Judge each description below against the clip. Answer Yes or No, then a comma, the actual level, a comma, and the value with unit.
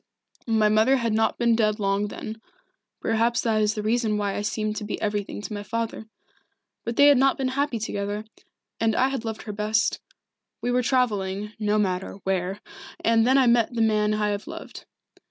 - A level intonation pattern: Yes, narrow, 2.0 semitones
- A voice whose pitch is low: No, high, 220 Hz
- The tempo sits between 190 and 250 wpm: Yes, average, 195 wpm